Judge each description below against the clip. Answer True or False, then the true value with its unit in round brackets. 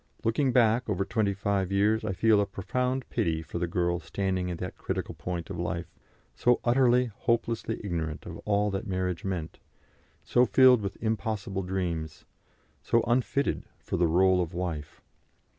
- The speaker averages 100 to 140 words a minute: False (160 wpm)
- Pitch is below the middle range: True (100 Hz)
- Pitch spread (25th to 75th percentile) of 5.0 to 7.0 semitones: False (4.3 semitones)